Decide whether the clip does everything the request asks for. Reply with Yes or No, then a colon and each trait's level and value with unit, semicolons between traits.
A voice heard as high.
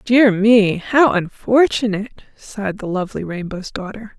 Yes: high, 210 Hz